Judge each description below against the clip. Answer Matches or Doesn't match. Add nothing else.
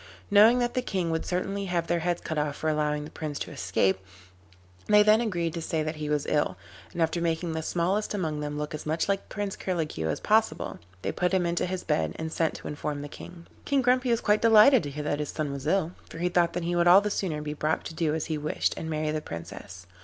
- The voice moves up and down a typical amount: Matches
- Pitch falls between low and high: Matches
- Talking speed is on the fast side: Matches